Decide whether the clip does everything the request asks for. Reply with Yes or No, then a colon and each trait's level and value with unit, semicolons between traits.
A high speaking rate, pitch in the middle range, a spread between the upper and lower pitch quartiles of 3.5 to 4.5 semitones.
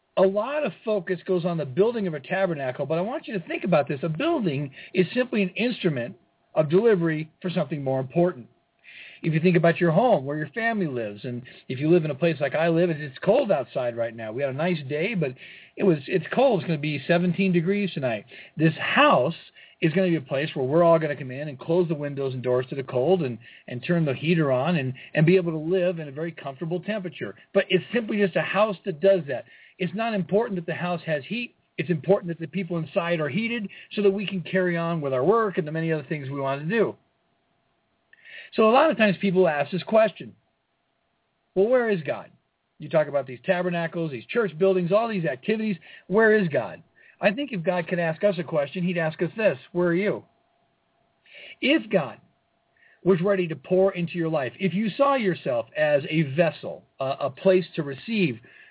Yes: fast, 225 wpm; medium, 175 Hz; average, 4.2 semitones